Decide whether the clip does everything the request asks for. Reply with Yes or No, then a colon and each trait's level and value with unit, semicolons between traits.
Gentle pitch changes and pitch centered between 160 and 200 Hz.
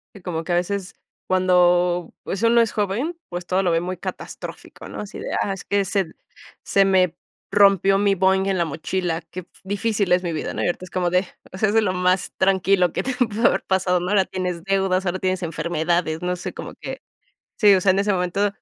Yes: narrow, 1.8 semitones; medium, 185 Hz